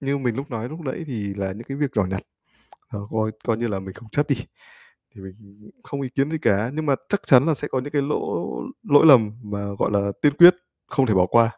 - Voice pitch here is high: No, low, 120 Hz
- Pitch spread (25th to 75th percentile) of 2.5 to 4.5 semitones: No, wide, 5.6 semitones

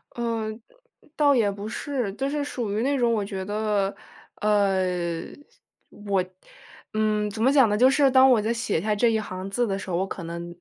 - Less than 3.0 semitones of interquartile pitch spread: No, average, 3.6 semitones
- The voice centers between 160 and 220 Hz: Yes, high, 210 Hz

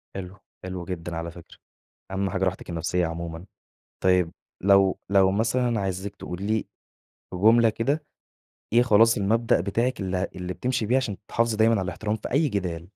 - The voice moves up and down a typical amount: Yes, average, 3.9 semitones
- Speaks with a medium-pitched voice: No, low, 100 Hz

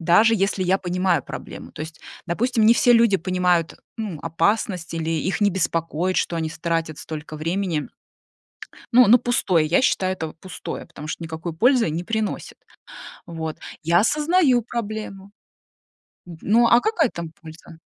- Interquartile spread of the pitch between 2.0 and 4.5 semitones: No, average, 5.0 semitones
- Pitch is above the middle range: No, medium, 180 Hz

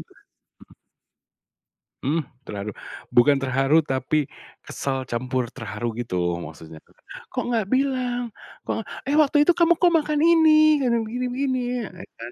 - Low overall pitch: No, high, 220 Hz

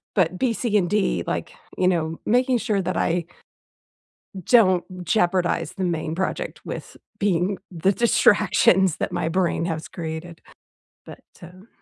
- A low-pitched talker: No, medium, 185 Hz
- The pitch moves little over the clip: No, average, 3.4 semitones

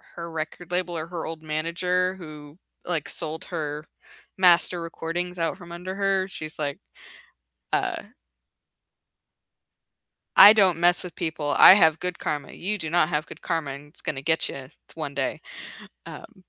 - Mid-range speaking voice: Yes, medium, 165 Hz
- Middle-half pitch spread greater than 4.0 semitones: No, narrow, 2.5 semitones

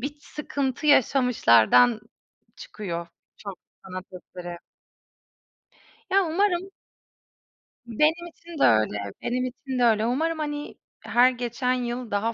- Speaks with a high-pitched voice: Yes, very high, 250 Hz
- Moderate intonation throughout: No, wide, 5.8 semitones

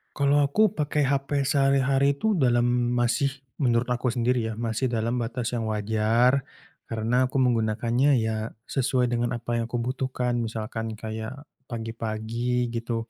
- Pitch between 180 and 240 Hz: No, low, 120 Hz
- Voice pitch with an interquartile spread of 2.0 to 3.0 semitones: Yes, narrow, 2.5 semitones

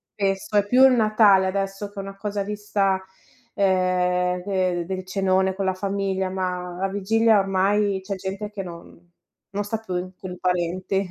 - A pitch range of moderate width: No, narrow, 1.6 semitones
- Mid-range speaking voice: No, high, 195 Hz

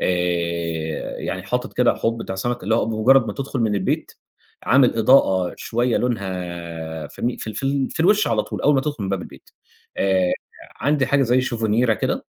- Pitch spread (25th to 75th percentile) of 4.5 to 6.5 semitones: Yes, average, 5.3 semitones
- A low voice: Yes, low, 115 Hz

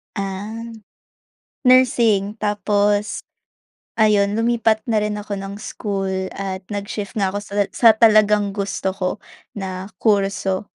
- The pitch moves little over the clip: Yes, narrow, 1.6 semitones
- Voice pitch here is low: No, high, 205 Hz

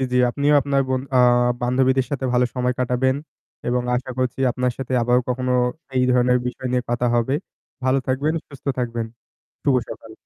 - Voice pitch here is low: Yes, low, 125 Hz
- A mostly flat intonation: Yes, narrow, 1.1 semitones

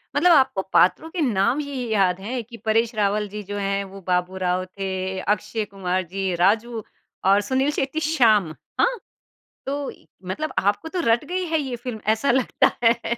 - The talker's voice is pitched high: Yes, high, 215 Hz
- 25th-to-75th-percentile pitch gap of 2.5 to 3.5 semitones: No, average, 5.3 semitones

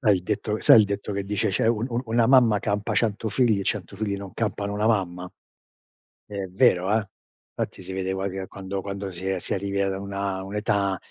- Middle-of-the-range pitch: No, low, 100 Hz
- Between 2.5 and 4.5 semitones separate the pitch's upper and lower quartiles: No, narrow, 1.9 semitones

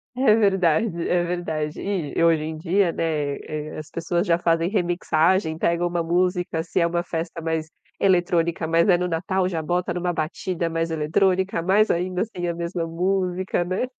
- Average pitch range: No, narrow, 2.0 semitones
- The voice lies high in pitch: No, medium, 175 Hz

